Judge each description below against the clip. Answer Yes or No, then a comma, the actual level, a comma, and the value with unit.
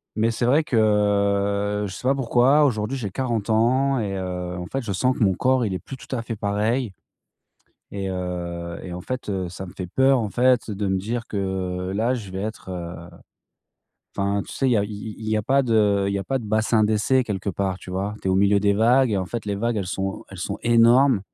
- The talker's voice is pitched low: Yes, low, 105 Hz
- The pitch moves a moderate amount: Yes, average, 3.7 semitones